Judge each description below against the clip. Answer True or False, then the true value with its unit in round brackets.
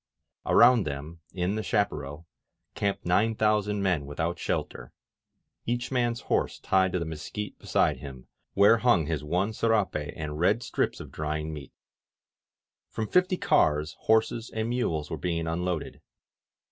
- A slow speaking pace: False (145 wpm)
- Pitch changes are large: True (6.1 semitones)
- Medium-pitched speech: False (90 Hz)